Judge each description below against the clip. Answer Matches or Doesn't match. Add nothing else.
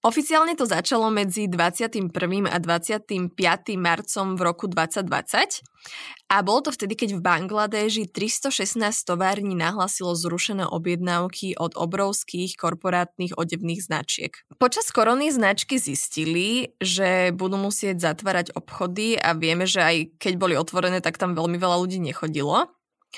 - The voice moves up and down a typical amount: Matches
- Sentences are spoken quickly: Doesn't match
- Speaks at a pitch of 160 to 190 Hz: Matches